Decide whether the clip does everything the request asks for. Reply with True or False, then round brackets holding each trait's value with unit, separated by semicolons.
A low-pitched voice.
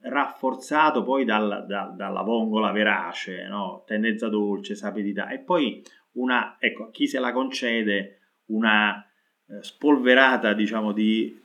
True (110 Hz)